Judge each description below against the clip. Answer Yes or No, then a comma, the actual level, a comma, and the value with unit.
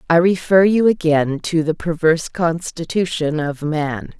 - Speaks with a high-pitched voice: No, medium, 165 Hz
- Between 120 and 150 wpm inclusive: Yes, average, 145 wpm